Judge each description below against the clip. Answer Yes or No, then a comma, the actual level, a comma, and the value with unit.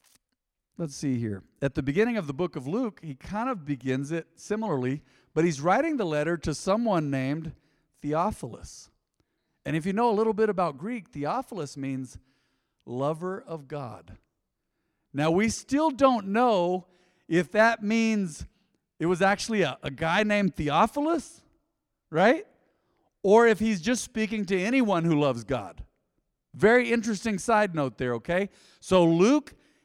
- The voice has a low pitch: No, medium, 180 Hz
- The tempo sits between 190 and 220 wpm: No, average, 150 wpm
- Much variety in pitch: Yes, wide, 6.9 semitones